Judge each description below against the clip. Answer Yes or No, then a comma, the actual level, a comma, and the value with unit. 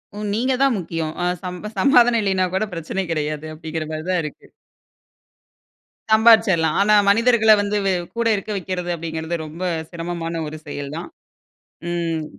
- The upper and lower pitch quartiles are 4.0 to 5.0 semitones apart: Yes, average, 4.6 semitones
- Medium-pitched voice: Yes, medium, 180 Hz